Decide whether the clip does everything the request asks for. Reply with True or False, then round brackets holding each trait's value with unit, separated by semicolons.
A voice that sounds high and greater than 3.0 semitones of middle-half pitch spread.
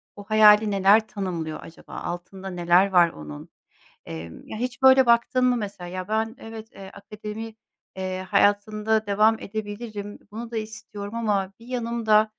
False (210 Hz; 2.6 semitones)